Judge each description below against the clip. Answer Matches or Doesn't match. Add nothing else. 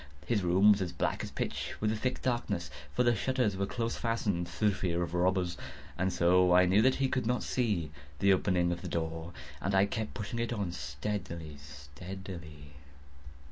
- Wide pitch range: Doesn't match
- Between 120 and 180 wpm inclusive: Doesn't match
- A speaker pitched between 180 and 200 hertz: Doesn't match